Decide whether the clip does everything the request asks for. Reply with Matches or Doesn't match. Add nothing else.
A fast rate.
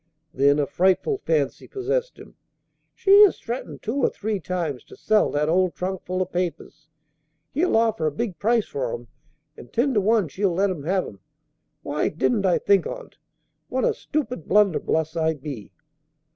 Doesn't match